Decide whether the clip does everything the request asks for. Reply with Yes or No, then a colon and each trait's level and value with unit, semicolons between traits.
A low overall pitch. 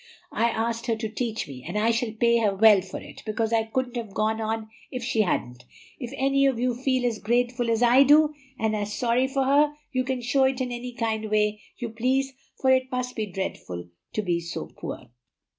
No: high, 235 Hz